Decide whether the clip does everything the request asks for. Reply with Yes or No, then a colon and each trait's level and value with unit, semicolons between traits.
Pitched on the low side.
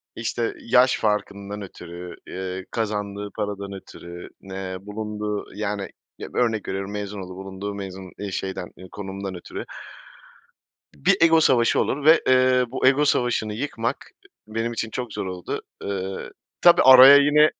Yes: low, 105 Hz